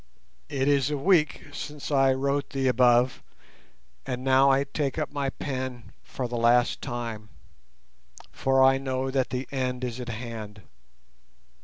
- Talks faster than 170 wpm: No, average, 150 wpm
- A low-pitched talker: Yes, low, 130 Hz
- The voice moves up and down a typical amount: No, narrow, 1.9 semitones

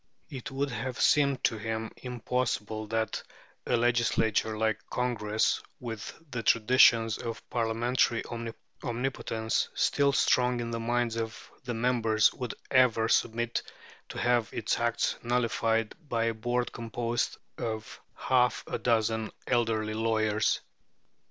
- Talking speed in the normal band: No, slow, 125 wpm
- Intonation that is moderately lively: No, narrow, 1.7 semitones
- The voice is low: Yes, low, 115 Hz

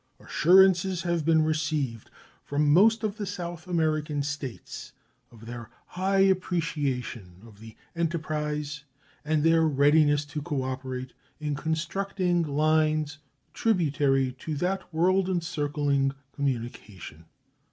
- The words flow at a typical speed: No, slow, 110 wpm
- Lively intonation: No, average, 3.5 semitones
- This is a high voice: No, medium, 155 Hz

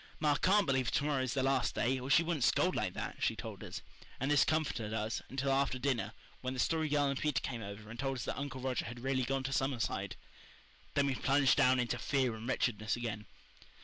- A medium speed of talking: No, fast, 230 wpm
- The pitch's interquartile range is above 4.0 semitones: No, narrow, 2.6 semitones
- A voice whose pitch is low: Yes, low, 130 Hz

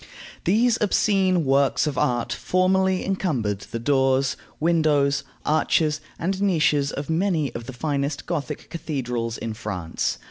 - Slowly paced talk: Yes, slow, 130 wpm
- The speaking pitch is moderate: Yes, medium, 150 Hz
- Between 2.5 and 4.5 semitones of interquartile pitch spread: No, average, 5.3 semitones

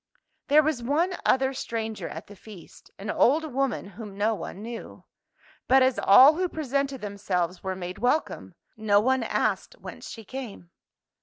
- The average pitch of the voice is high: Yes, high, 235 Hz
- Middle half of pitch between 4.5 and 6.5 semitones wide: Yes, average, 5.0 semitones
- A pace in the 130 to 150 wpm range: No, average, 160 wpm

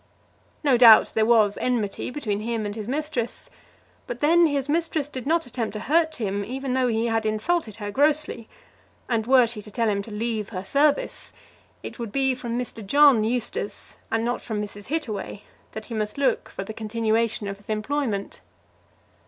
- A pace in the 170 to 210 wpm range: Yes, average, 185 wpm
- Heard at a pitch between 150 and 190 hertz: No, high, 230 Hz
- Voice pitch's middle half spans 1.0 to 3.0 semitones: No, average, 4.0 semitones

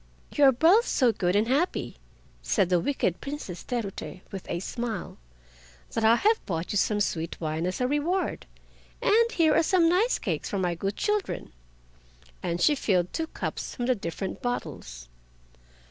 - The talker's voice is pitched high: Yes, high, 225 Hz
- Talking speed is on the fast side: No, average, 165 wpm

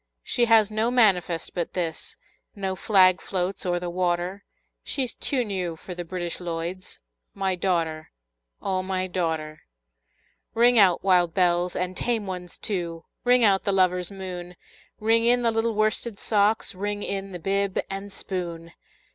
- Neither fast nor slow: Yes, average, 155 wpm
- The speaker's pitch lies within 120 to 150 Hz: No, medium, 185 Hz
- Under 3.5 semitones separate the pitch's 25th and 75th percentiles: Yes, average, 2.7 semitones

